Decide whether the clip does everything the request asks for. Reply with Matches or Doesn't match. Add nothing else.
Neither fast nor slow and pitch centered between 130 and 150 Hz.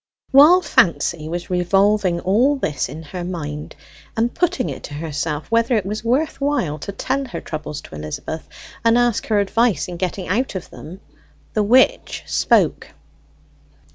Doesn't match